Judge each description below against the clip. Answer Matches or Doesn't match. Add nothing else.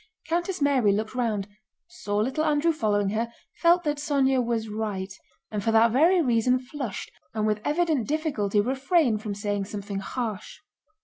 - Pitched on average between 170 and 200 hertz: Doesn't match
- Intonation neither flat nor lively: Doesn't match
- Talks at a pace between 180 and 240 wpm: Doesn't match